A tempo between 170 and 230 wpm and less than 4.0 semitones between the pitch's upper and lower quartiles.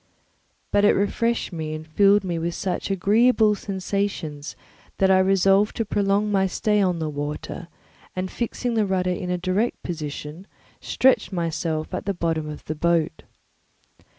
No: average, 155 wpm; average, 3.6 semitones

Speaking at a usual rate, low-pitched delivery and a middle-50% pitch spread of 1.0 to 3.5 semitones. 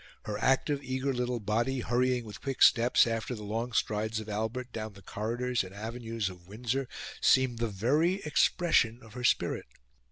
Yes: average, 170 wpm; low, 115 Hz; average, 2.8 semitones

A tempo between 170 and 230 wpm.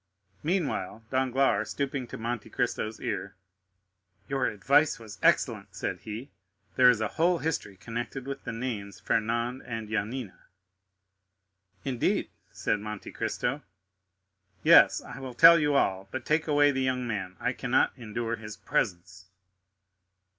No: slow, 135 wpm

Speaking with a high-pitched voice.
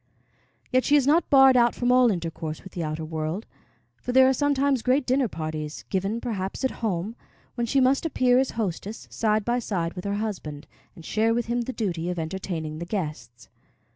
Yes: high, 215 Hz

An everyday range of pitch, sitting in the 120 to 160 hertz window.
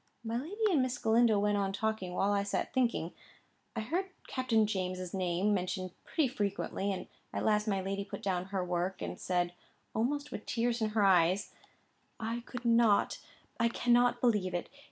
No: average, 4.0 semitones; high, 210 Hz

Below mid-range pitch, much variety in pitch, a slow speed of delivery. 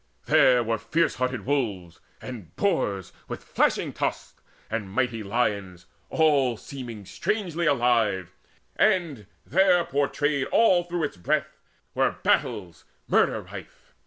Yes: low, 125 Hz; wide, 6.9 semitones; slow, 120 wpm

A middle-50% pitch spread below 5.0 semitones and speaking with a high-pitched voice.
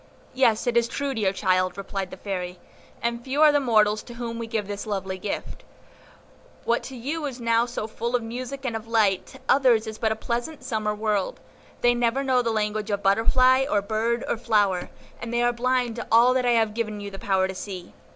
Yes: average, 2.8 semitones; high, 230 Hz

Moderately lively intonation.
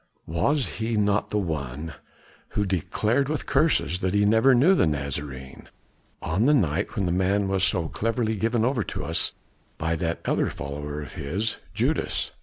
No: wide, 5.9 semitones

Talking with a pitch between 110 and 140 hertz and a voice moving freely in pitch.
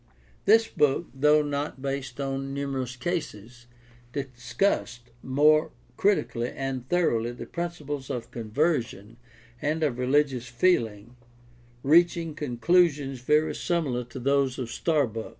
No: low, 135 Hz; average, 3.8 semitones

